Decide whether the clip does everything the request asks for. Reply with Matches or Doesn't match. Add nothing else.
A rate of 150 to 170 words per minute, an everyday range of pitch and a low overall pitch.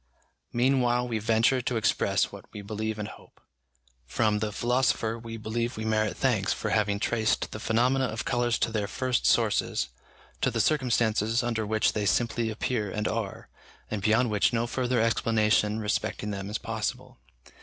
Doesn't match